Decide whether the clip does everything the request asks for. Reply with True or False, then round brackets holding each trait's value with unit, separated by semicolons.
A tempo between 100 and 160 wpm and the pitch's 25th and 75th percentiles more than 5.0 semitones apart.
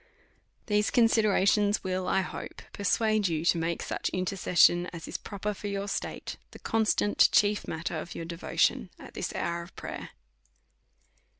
False (155 wpm; 3.2 semitones)